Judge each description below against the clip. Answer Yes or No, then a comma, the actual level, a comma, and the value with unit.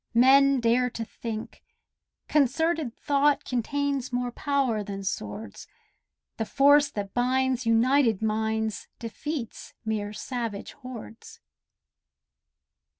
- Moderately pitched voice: No, high, 245 Hz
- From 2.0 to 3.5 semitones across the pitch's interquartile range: No, average, 3.9 semitones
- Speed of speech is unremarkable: No, slow, 95 wpm